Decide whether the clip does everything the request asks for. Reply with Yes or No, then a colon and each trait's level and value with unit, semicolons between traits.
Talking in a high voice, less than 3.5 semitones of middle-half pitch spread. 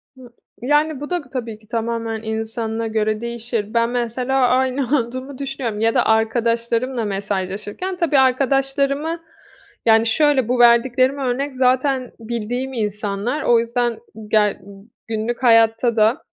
Yes: high, 235 Hz; average, 2.9 semitones